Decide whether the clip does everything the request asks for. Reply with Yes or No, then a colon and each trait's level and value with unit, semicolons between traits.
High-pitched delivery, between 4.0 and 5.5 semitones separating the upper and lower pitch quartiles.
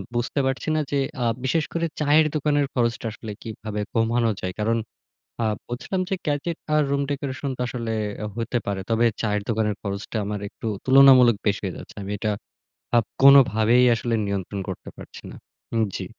No: low, 115 Hz; average, 4.5 semitones